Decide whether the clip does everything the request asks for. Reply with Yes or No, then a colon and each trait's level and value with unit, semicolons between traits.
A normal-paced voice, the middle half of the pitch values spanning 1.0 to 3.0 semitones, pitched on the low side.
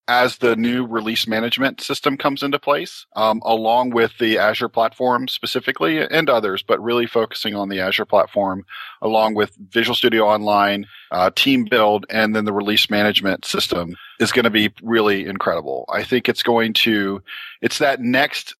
Yes: average, 170 wpm; narrow, 2.5 semitones; low, 115 Hz